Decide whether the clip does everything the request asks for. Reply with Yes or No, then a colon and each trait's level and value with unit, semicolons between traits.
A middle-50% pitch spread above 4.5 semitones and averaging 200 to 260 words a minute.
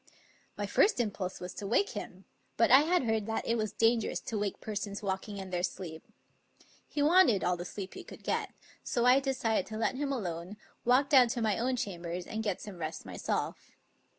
Yes: average, 4.9 semitones; fast, 205 wpm